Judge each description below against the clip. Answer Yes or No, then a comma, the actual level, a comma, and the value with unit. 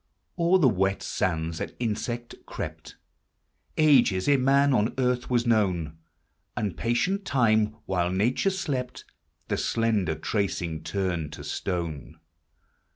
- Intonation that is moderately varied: No, wide, 5.7 semitones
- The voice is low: Yes, low, 110 Hz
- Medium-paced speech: No, slow, 125 wpm